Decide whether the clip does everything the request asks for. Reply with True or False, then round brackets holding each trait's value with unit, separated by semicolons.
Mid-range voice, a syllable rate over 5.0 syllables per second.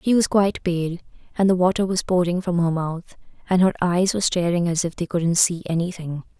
True (175 Hz; 5.6 syllables/s)